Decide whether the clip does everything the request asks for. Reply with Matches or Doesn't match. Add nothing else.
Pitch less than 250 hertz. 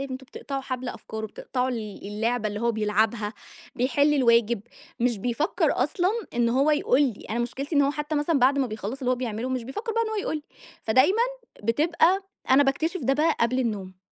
Doesn't match